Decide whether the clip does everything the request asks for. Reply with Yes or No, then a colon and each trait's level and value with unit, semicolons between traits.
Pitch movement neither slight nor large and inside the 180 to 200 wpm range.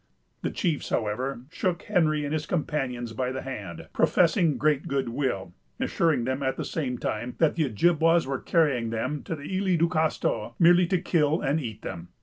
Yes: average, 4.8 semitones; average, 185 wpm